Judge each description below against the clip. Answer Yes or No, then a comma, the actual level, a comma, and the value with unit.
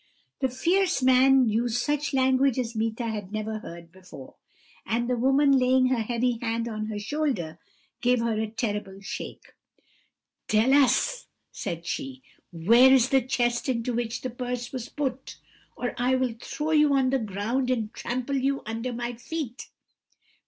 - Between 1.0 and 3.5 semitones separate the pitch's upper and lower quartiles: Yes, average, 2.9 semitones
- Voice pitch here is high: Yes, high, 245 Hz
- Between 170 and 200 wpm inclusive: No, average, 160 wpm